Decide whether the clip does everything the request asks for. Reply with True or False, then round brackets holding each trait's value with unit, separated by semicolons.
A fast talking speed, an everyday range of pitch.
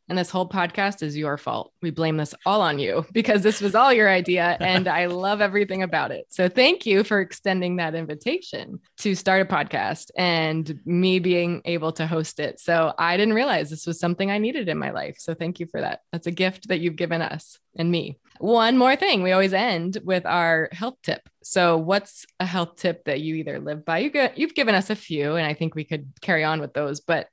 True (230 wpm; 3.3 semitones)